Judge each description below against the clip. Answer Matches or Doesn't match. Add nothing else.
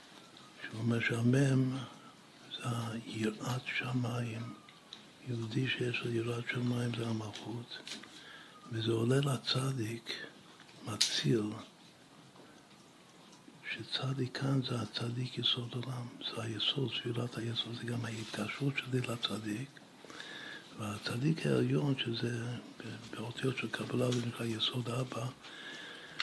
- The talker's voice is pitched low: Matches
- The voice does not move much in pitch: Matches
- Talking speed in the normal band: Doesn't match